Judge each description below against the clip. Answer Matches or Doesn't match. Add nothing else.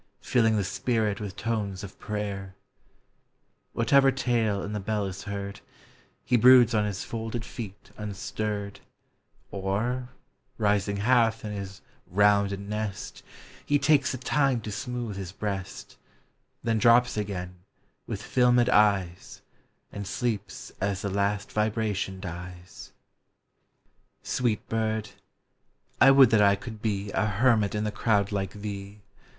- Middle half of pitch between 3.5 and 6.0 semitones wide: Doesn't match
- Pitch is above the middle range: Doesn't match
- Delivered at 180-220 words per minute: Doesn't match